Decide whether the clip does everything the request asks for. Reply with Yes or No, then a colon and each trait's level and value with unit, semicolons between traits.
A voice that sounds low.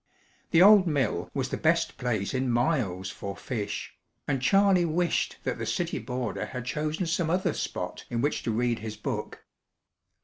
Yes: low, 130 Hz